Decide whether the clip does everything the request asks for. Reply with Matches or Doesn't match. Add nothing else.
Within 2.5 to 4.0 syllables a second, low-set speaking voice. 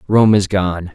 Matches